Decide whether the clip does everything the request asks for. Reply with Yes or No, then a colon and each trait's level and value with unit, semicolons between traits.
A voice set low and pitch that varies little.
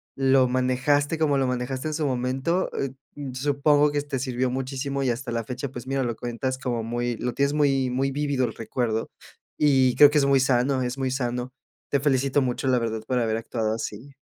Yes: low, 130 Hz; narrow, 2.2 semitones